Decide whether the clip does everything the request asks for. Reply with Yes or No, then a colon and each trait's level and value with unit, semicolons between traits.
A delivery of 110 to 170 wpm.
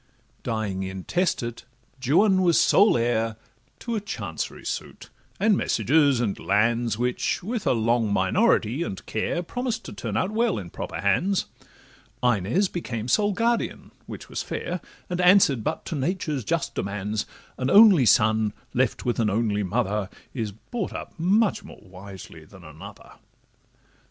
Yes: average, 145 wpm